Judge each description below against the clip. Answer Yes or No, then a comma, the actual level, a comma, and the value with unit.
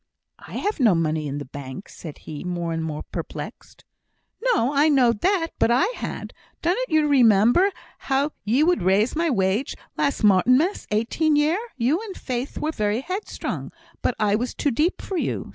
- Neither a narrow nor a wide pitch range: No, wide, 8.0 semitones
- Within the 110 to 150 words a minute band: No, average, 180 wpm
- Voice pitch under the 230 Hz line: No, very high, 255 Hz